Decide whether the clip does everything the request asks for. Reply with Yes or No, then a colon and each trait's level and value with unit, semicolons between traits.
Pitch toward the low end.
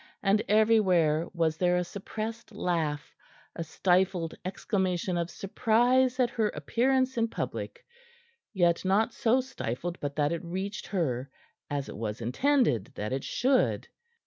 No: medium, 185 Hz